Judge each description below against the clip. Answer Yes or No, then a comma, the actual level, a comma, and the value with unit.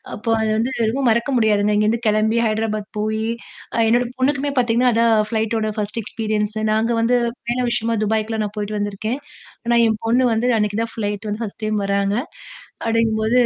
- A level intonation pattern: Yes, narrow, 1.5 semitones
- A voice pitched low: No, high, 220 Hz